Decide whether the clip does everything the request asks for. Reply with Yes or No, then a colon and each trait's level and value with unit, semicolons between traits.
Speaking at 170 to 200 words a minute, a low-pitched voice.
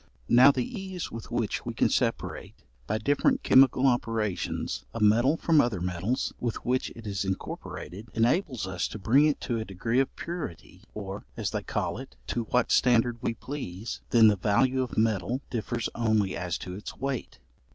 Yes: average, 180 wpm; low, 115 Hz